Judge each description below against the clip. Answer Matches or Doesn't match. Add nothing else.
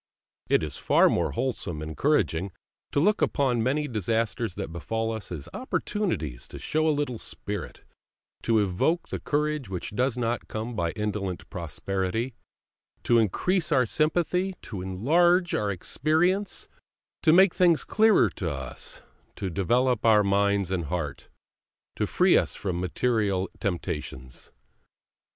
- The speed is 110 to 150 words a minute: Matches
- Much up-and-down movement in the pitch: Matches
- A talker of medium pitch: Doesn't match